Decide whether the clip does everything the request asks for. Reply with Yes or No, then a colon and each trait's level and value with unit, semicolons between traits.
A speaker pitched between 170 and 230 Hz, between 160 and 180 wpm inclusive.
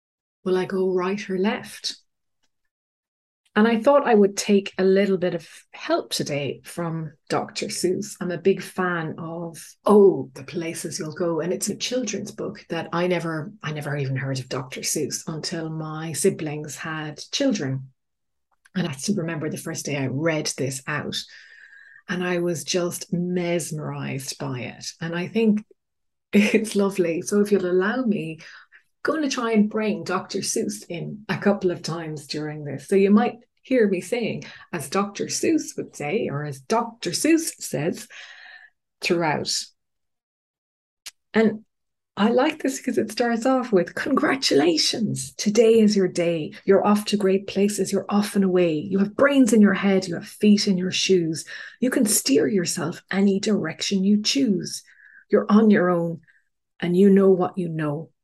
Yes: high, 190 Hz; average, 170 wpm